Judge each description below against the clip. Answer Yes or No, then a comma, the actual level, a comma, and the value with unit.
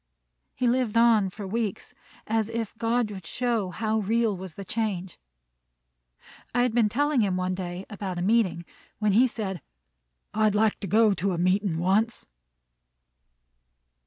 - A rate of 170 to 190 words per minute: No, average, 155 wpm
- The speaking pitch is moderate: No, high, 210 Hz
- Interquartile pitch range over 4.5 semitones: No, average, 3.3 semitones